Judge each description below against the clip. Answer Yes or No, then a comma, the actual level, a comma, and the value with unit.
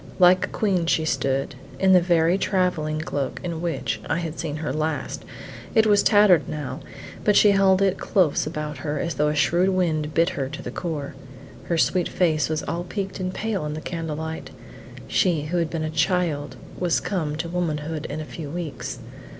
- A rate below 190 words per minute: No, average, 200 wpm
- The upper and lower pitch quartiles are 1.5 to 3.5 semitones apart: Yes, average, 3.1 semitones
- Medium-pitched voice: Yes, medium, 165 Hz